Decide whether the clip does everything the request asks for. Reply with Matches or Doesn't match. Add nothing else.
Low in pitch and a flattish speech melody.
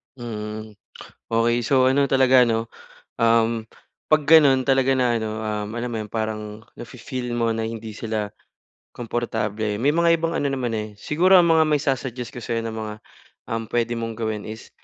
Doesn't match